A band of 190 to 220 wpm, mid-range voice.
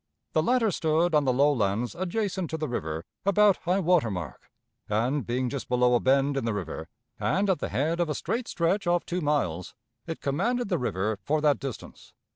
Yes: fast, 205 wpm; medium, 150 Hz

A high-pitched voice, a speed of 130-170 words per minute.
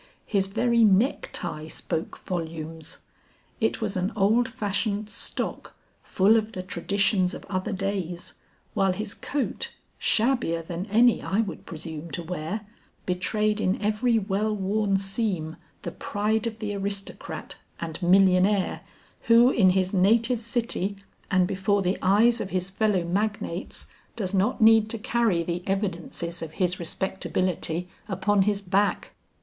Yes: high, 195 Hz; average, 140 wpm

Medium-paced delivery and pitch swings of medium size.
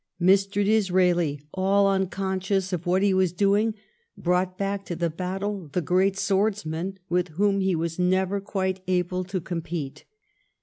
No: average, 145 wpm; narrow, 1.7 semitones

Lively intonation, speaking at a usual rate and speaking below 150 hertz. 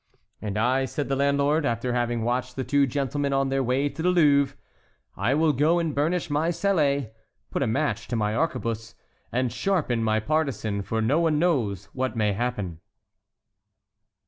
No: average, 4.2 semitones; average, 170 wpm; low, 135 Hz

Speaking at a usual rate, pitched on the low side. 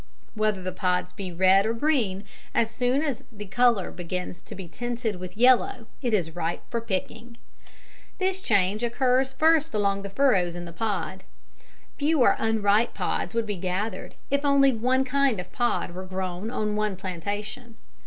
No: average, 165 wpm; high, 215 Hz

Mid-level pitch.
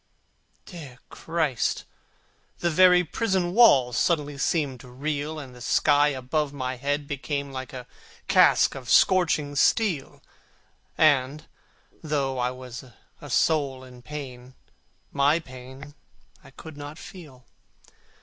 Yes: medium, 145 Hz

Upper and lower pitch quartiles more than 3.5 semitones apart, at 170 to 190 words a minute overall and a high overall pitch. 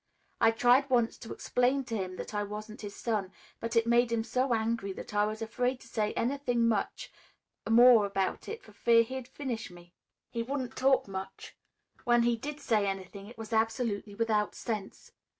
No: average, 2.8 semitones; average, 185 wpm; high, 230 Hz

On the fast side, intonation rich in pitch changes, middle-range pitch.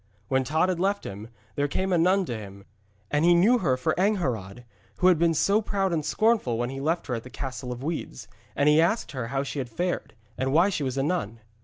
Yes: fast, 240 wpm; wide, 6.2 semitones; medium, 150 Hz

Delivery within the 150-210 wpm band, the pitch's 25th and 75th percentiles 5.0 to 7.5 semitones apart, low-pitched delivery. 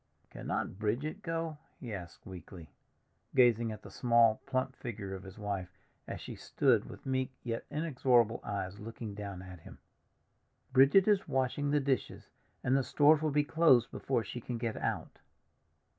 Yes: average, 160 wpm; wide, 5.4 semitones; low, 120 Hz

